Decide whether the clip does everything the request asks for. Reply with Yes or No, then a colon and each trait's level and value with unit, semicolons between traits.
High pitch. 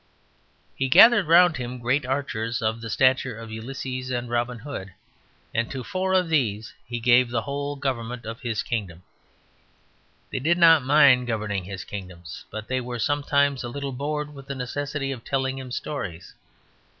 No: low, 125 Hz